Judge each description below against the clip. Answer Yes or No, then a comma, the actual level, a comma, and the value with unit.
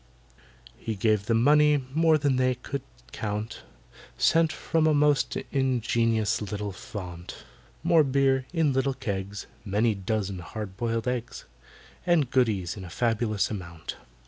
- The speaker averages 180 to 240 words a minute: No, slow, 135 wpm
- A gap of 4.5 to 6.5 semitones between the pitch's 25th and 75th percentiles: Yes, average, 5.0 semitones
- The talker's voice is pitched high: No, low, 115 Hz